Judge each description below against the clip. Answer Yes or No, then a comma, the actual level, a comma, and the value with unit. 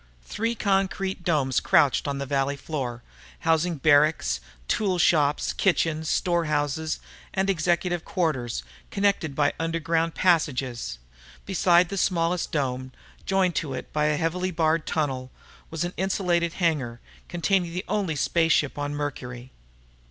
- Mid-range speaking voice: Yes, medium, 160 Hz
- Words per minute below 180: Yes, slow, 135 wpm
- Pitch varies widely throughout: No, average, 3.7 semitones